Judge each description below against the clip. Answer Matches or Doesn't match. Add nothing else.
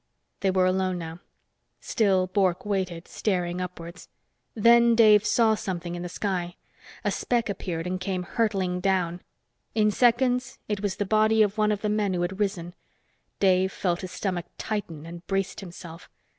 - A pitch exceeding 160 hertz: Matches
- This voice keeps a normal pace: Matches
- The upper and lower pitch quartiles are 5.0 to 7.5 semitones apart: Doesn't match